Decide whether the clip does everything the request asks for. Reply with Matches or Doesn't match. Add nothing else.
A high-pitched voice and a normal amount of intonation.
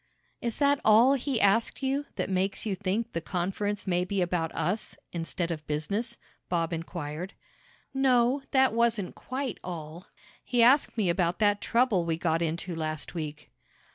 Doesn't match